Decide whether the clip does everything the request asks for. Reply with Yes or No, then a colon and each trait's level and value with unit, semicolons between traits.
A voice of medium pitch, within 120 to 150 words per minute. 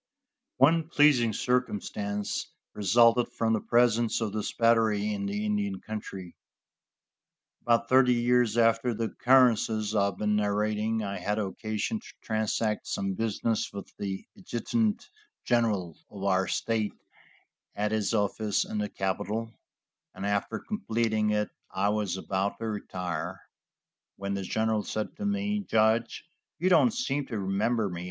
No: low, 110 Hz; average, 140 wpm